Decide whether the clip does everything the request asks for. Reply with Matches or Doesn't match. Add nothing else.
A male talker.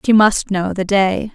Doesn't match